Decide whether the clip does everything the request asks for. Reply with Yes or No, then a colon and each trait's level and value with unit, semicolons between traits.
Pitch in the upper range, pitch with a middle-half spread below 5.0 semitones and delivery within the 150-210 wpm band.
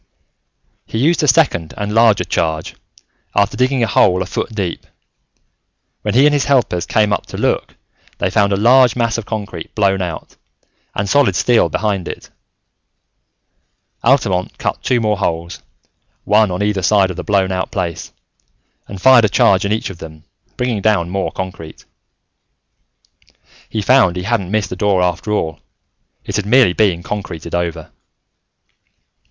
No: low, 100 Hz; average, 3.7 semitones; average, 160 wpm